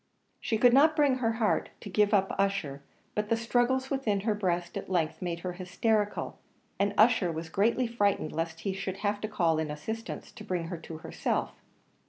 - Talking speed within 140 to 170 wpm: No, average, 195 wpm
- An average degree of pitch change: Yes, average, 4.5 semitones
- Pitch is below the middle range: No, high, 200 Hz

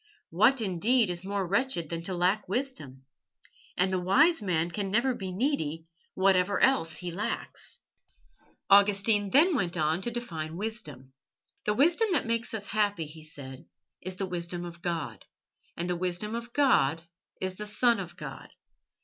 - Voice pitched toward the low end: No, high, 190 Hz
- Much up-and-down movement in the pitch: No, average, 4.9 semitones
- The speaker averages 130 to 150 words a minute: No, average, 160 wpm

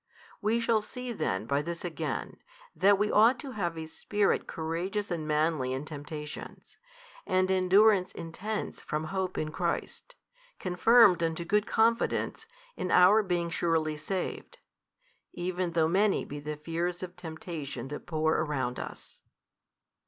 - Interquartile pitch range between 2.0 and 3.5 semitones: No, average, 4.3 semitones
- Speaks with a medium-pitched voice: Yes, medium, 175 Hz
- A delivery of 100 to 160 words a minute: Yes, average, 140 wpm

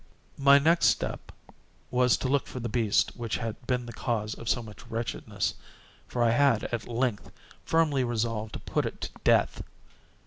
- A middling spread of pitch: No, narrow, 2.2 semitones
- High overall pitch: No, low, 120 Hz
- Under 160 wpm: No, average, 175 wpm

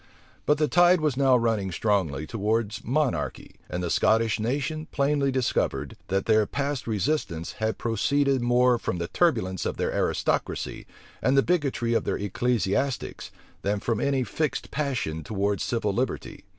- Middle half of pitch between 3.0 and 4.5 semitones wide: No, wide, 5.4 semitones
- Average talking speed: Yes, average, 150 wpm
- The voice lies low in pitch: Yes, low, 120 Hz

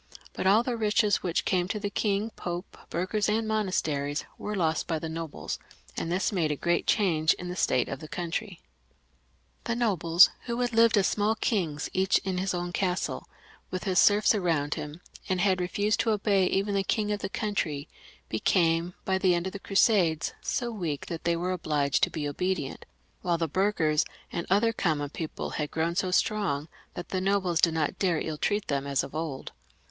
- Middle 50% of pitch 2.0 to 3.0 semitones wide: No, average, 4.0 semitones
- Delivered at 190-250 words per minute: Yes, average, 200 wpm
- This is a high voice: No, medium, 180 Hz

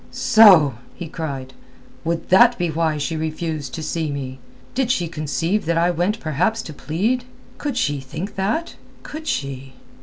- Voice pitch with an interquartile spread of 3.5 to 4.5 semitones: No, average, 5.3 semitones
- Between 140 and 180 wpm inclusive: Yes, average, 160 wpm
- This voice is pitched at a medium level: Yes, medium, 165 Hz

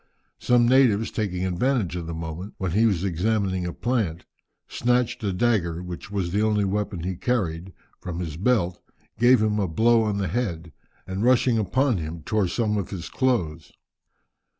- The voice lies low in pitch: Yes, low, 100 Hz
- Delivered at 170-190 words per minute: Yes, average, 175 wpm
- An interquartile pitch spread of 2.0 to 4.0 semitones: No, average, 4.7 semitones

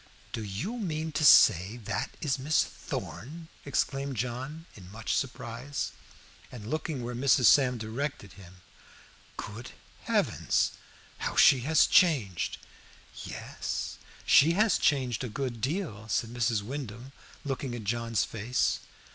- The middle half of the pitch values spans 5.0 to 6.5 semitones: No, average, 4.4 semitones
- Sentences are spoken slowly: Yes, slow, 130 wpm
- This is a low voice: Yes, low, 125 Hz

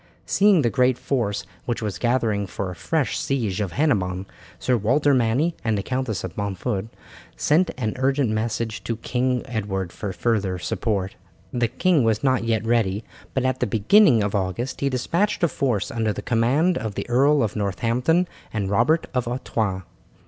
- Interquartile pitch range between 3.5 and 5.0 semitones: Yes, average, 4.2 semitones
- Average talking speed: Yes, average, 175 wpm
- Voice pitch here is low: Yes, low, 115 Hz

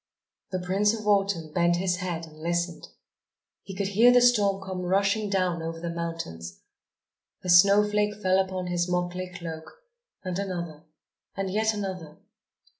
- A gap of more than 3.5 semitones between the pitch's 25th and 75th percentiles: No, narrow, 2.6 semitones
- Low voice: No, medium, 185 Hz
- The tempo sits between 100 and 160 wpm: Yes, average, 150 wpm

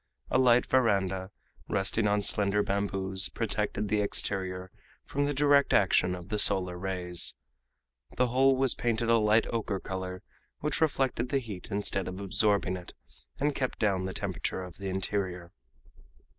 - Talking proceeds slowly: No, average, 155 wpm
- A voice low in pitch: Yes, low, 100 Hz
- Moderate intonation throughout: Yes, average, 4.1 semitones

